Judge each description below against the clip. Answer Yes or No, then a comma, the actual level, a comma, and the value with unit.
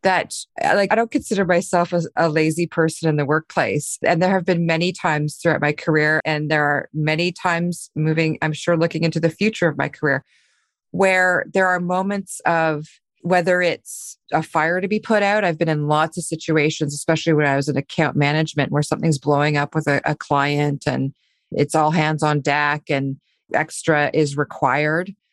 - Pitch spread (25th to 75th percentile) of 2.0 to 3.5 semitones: Yes, average, 2.9 semitones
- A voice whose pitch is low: No, medium, 160 Hz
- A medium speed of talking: Yes, average, 190 wpm